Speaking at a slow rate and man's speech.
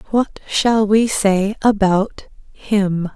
No: slow, 115 wpm; female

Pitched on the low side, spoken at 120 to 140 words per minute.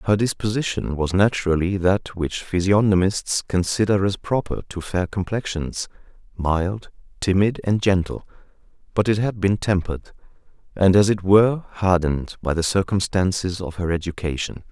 Yes: very low, 95 Hz; slow, 135 wpm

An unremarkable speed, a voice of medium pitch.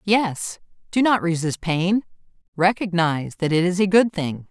Yes: average, 160 wpm; medium, 180 Hz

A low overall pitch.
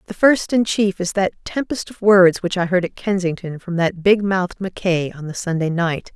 No: medium, 185 Hz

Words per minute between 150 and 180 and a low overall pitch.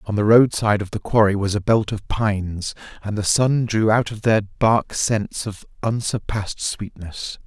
No: average, 195 wpm; low, 105 Hz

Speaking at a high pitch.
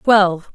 Yes: high, 195 Hz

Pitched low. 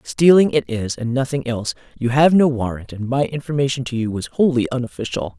Yes: low, 125 Hz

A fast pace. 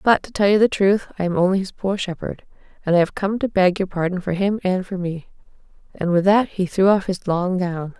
Yes: fast, 255 wpm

